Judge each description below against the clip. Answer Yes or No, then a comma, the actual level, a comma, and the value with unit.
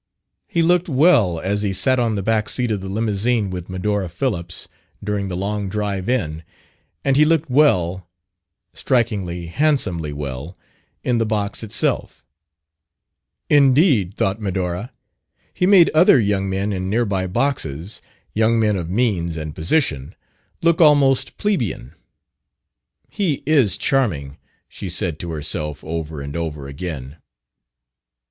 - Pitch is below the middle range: Yes, low, 100 Hz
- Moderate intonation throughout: No, wide, 6.5 semitones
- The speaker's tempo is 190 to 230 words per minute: No, slow, 135 wpm